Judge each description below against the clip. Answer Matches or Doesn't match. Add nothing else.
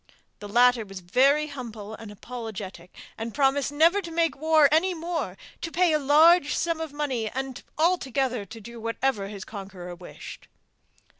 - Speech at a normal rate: Matches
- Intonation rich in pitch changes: Matches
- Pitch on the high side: Matches